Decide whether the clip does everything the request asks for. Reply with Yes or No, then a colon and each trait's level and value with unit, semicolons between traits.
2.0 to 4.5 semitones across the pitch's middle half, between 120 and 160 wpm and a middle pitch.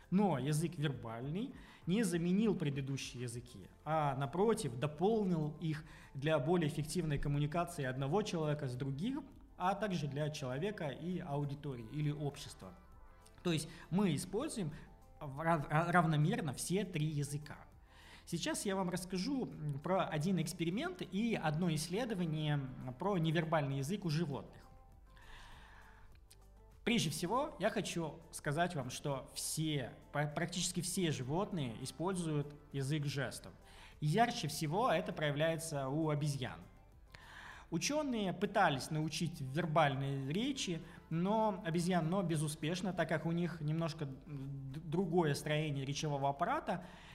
No: average, 4.1 semitones; slow, 110 wpm; medium, 155 Hz